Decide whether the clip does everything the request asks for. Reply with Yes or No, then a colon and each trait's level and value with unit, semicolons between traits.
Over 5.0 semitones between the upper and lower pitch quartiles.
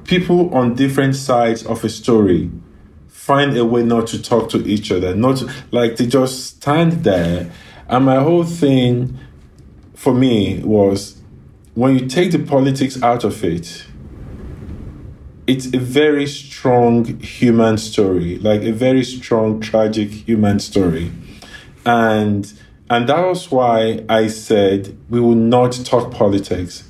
No: average, 3.8 semitones